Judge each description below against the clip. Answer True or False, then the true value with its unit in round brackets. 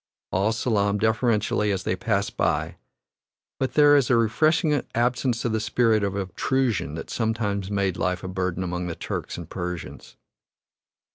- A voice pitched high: False (105 Hz)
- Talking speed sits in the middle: True (155 wpm)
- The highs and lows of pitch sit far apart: False (4.2 semitones)